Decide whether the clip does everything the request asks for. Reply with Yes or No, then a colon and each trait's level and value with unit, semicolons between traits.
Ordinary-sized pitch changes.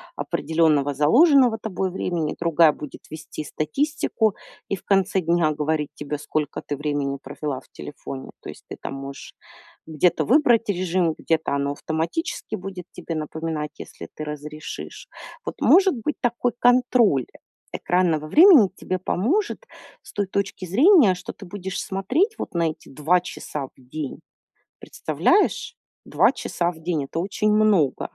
No: wide, 5.9 semitones